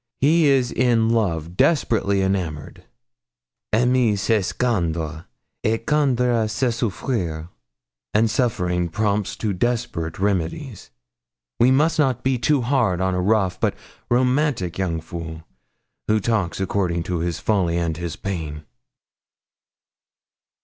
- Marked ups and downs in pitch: Yes, wide, 5.9 semitones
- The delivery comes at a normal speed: No, slow, 120 wpm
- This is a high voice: No, low, 105 Hz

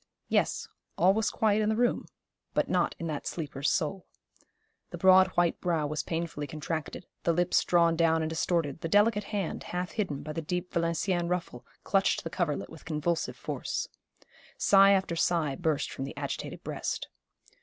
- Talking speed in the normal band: Yes, average, 170 wpm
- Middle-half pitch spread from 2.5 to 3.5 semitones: Yes, average, 3.1 semitones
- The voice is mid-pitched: Yes, medium, 170 Hz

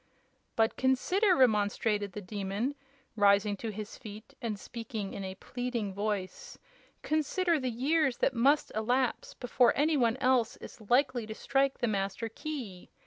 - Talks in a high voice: Yes, high, 230 Hz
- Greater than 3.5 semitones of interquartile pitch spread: Yes, average, 4.2 semitones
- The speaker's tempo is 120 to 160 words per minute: Yes, average, 145 wpm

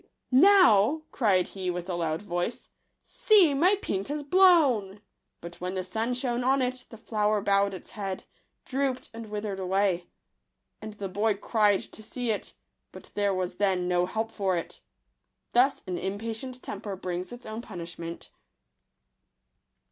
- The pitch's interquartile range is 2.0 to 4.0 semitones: No, average, 4.9 semitones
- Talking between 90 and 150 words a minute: No, average, 165 wpm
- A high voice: Yes, high, 210 Hz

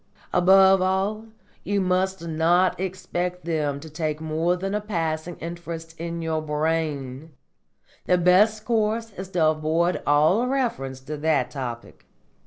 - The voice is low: No, medium, 170 Hz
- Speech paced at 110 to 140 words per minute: Yes, slow, 135 wpm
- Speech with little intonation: No, average, 3.4 semitones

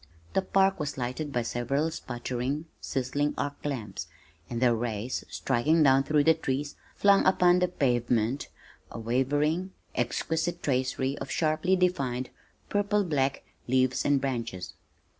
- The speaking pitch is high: No, medium, 140 Hz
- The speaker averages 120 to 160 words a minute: Yes, slow, 135 wpm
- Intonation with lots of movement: No, average, 4.7 semitones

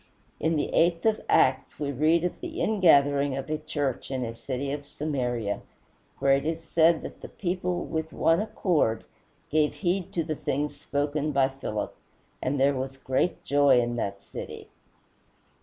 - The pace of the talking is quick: No, average, 170 wpm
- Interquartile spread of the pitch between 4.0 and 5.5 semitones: No, average, 3.4 semitones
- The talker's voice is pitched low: No, medium, 145 Hz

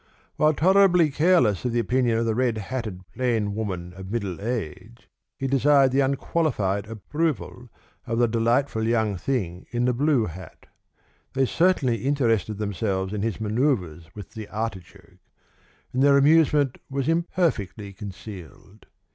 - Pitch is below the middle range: Yes, low, 115 Hz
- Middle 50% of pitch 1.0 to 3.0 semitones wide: No, average, 5.2 semitones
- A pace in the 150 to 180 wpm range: No, average, 140 wpm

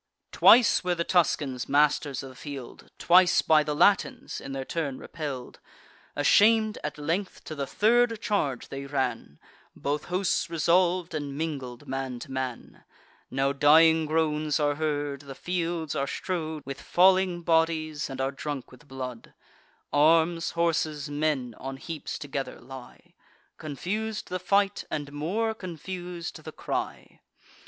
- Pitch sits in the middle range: Yes, medium, 155 Hz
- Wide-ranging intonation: No, average, 4.0 semitones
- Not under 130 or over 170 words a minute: Yes, average, 140 wpm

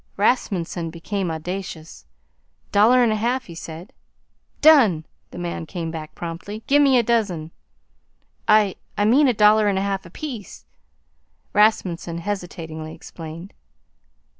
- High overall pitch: Yes, high, 195 Hz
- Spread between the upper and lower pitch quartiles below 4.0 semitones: No, average, 4.6 semitones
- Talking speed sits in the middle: No, slow, 125 wpm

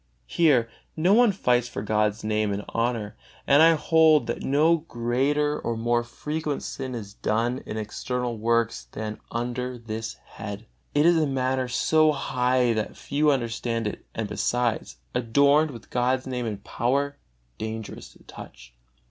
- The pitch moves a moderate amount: Yes, average, 4.1 semitones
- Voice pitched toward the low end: Yes, low, 125 Hz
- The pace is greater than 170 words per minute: No, average, 155 wpm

